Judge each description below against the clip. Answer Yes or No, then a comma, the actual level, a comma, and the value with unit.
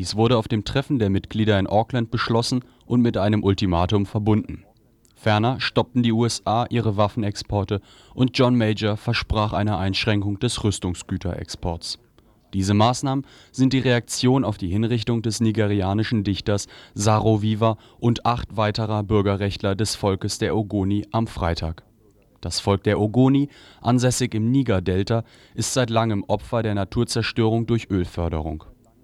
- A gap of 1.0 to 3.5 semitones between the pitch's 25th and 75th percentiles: Yes, average, 2.8 semitones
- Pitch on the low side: Yes, low, 110 Hz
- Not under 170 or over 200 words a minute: No, average, 140 wpm